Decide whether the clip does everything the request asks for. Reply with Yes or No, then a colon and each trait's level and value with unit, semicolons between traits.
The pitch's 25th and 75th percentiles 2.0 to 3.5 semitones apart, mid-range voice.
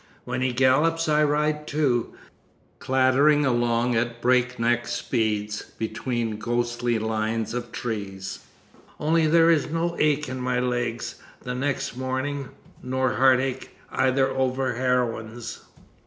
No: narrow, 2.6 semitones; low, 125 Hz